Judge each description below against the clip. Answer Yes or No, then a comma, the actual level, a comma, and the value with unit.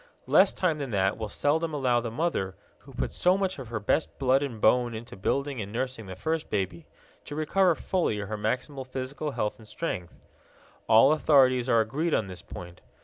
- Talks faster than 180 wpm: Yes, average, 195 wpm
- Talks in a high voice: No, low, 125 Hz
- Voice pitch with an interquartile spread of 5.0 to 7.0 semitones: Yes, wide, 5.5 semitones